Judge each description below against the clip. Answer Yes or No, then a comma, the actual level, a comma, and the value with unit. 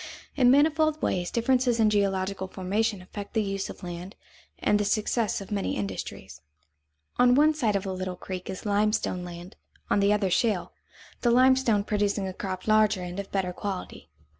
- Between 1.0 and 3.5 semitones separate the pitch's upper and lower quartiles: Yes, average, 3.2 semitones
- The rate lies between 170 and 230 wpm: Yes, average, 175 wpm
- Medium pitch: No, high, 205 Hz